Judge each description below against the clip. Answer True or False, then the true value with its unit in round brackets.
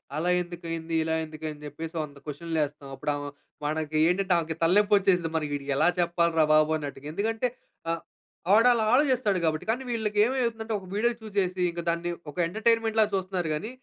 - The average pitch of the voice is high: False (175 Hz)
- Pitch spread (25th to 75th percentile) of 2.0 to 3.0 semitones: False (5.2 semitones)